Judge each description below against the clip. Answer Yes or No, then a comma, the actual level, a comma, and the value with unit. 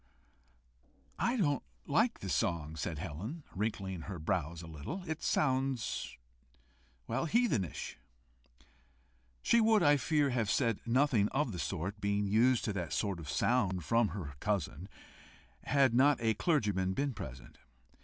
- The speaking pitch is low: Yes, low, 110 Hz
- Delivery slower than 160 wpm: Yes, average, 140 wpm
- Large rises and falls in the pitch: Yes, wide, 7.4 semitones